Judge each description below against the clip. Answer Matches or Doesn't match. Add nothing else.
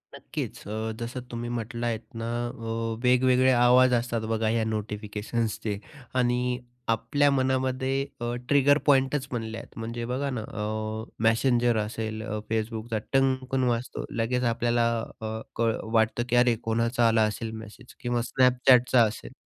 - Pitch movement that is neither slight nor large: Doesn't match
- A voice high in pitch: Doesn't match